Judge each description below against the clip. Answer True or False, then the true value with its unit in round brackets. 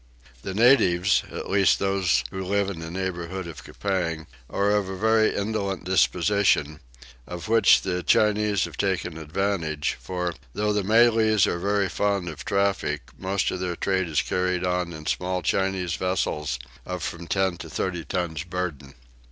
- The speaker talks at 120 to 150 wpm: False (160 wpm)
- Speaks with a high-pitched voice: False (95 Hz)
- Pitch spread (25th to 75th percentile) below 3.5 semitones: True (2.4 semitones)